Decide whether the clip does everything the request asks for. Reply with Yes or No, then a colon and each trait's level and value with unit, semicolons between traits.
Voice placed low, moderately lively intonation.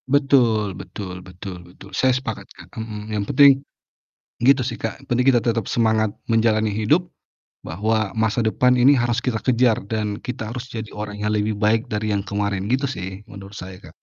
Yes: low, 110 Hz; average, 3.1 semitones